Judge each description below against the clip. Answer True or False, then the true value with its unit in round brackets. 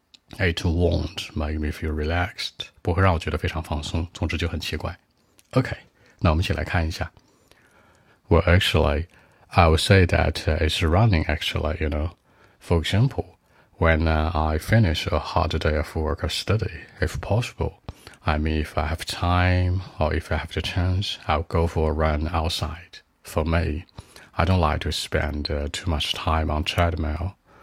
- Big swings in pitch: False (3.0 semitones)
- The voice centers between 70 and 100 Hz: True (85 Hz)